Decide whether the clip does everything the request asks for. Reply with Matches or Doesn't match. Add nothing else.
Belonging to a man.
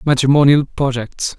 Matches